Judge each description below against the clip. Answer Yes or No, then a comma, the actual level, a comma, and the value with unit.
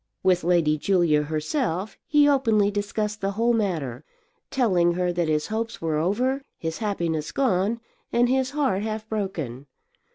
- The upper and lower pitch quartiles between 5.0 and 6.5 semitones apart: Yes, wide, 5.6 semitones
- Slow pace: No, average, 150 wpm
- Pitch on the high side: Yes, high, 200 Hz